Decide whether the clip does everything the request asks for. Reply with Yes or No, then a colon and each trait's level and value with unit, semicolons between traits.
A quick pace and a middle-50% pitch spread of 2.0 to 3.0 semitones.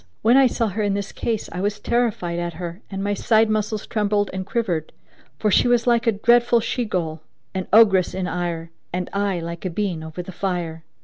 No: fast, 210 wpm; average, 3.8 semitones